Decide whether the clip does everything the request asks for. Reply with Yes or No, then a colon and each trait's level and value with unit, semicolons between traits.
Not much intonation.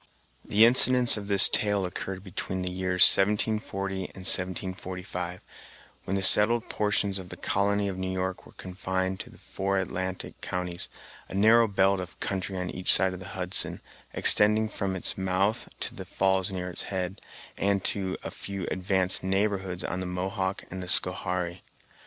Yes: narrow, 1.4 semitones